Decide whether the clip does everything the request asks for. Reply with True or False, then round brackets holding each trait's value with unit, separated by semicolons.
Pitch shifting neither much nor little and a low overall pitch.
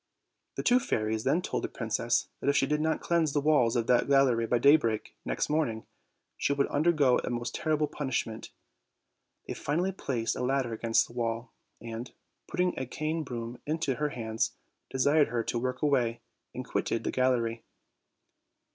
True (4.4 semitones; 130 Hz)